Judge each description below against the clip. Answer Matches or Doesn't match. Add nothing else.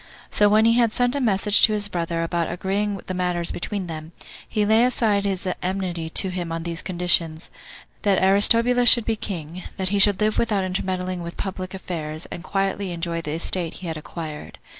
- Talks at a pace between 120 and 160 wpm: Doesn't match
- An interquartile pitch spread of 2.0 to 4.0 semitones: Matches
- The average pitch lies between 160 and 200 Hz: Matches